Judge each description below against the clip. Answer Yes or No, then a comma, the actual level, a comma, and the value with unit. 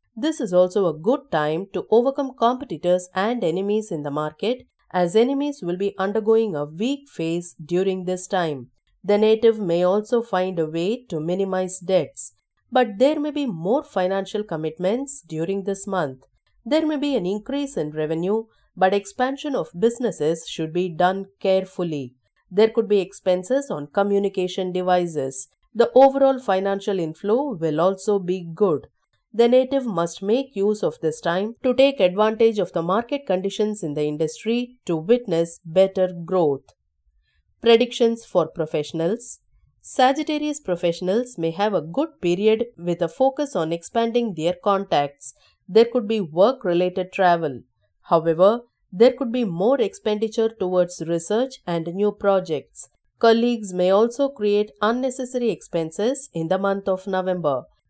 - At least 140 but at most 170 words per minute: Yes, average, 145 wpm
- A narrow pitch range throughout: No, average, 5.2 semitones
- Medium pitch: No, high, 195 Hz